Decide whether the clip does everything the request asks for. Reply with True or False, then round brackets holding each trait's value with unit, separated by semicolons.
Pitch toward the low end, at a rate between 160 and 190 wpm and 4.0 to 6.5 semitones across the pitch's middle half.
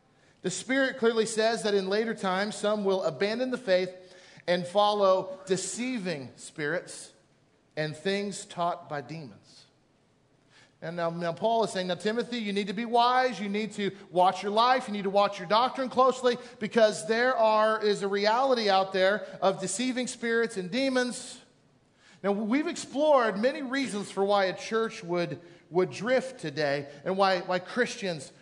False (200 Hz; 165 wpm; 4.3 semitones)